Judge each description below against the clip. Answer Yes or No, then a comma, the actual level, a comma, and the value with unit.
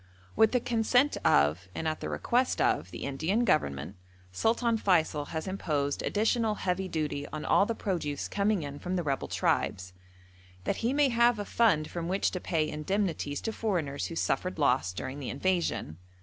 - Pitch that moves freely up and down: Yes, wide, 7.0 semitones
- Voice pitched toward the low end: No, medium, 175 Hz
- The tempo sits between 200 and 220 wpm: No, average, 180 wpm